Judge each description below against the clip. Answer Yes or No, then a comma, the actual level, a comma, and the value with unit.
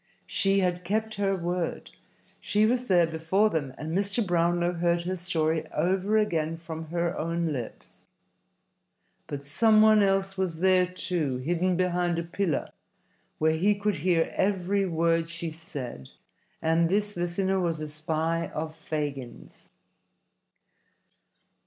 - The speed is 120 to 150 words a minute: Yes, slow, 135 wpm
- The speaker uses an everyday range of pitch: Yes, average, 3.0 semitones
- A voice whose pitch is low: No, medium, 175 Hz